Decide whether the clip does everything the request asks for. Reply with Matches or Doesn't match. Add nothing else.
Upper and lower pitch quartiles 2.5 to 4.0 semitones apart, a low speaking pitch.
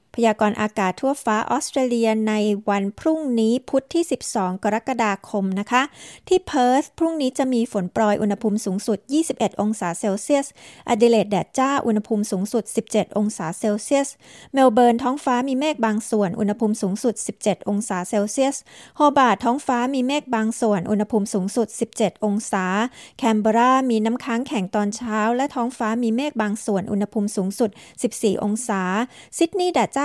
Doesn't match